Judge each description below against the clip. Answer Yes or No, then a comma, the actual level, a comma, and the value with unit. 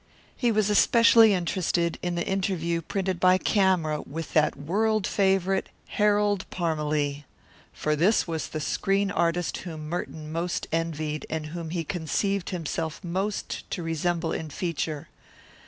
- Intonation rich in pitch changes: No, average, 3.4 semitones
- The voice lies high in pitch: No, medium, 170 Hz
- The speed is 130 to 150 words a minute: Yes, average, 140 wpm